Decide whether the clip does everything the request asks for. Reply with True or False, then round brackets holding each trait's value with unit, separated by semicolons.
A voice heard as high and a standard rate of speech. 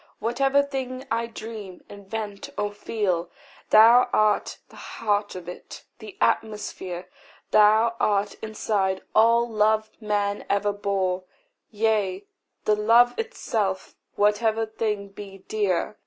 False (210 Hz; 115 wpm)